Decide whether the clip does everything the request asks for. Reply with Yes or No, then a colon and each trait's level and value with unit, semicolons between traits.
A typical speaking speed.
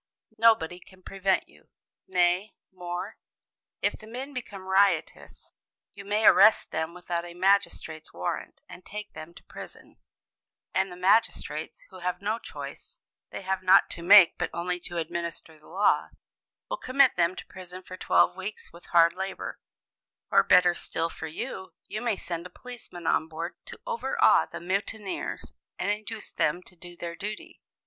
Yes: average, 165 wpm